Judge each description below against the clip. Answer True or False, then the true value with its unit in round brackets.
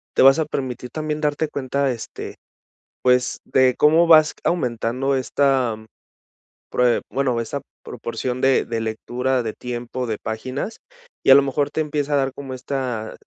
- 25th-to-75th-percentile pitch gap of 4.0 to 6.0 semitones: False (2.5 semitones)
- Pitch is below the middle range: True (130 Hz)